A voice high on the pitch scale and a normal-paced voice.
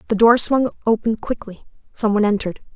Yes: high, 220 Hz; average, 150 wpm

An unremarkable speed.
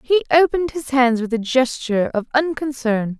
Yes: average, 170 wpm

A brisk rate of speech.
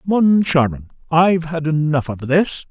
No: slow, 135 wpm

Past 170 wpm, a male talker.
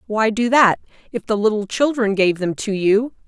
No: average, 200 wpm; female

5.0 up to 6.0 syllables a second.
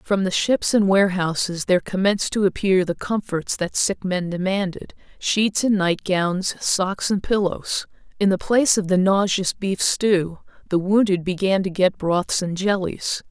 No: 4.4 syllables/s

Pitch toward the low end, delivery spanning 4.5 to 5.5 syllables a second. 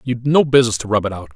No: low, 120 Hz; 7.4 syllables/s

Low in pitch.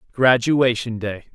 Yes: low, 120 Hz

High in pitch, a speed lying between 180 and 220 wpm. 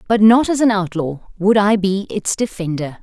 Yes: high, 200 Hz; average, 200 wpm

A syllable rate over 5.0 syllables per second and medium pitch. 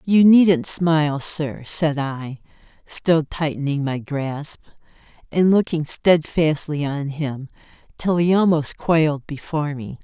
No: 3.8 syllables/s; medium, 155 Hz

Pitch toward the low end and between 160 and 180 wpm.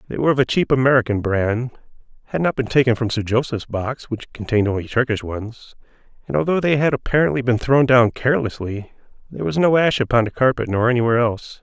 No: low, 120 Hz; average, 200 wpm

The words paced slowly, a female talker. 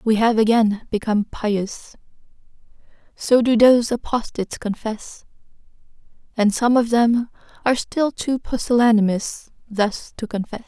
Yes: slow, 110 wpm; female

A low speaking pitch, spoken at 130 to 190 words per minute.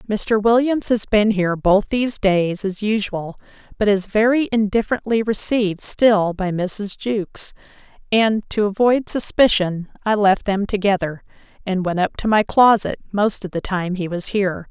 No: high, 205 Hz; average, 165 wpm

